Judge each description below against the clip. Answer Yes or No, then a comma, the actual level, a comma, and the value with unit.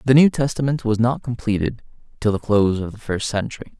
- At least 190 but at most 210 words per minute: Yes, fast, 205 wpm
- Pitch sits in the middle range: No, low, 115 Hz